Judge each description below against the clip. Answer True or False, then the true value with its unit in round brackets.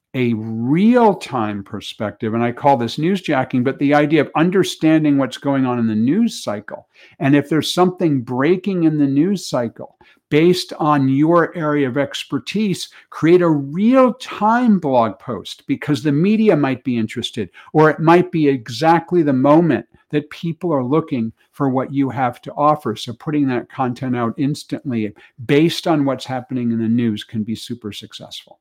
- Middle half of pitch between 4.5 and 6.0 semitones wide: True (4.8 semitones)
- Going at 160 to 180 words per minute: True (170 wpm)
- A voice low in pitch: False (145 Hz)